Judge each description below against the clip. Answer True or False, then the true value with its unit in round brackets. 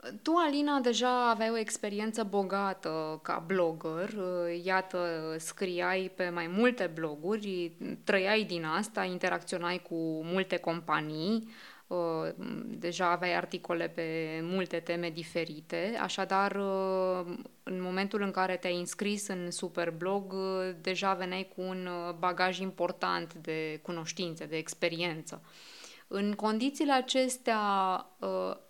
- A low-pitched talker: False (185 Hz)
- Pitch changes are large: False (2.7 semitones)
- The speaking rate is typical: False (105 wpm)